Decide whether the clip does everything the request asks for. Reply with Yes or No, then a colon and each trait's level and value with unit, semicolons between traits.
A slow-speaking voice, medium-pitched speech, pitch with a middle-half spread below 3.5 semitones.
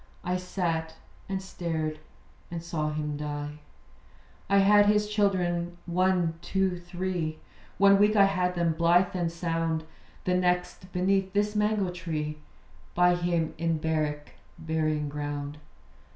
Yes: slow, 130 wpm; medium, 175 Hz; average, 2.9 semitones